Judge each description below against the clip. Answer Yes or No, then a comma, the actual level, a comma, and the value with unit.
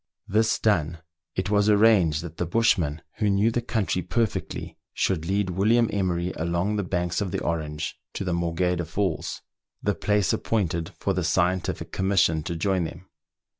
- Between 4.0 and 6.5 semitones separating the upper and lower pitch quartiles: No, average, 3.4 semitones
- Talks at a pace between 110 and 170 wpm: Yes, average, 165 wpm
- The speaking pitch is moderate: No, very low, 90 Hz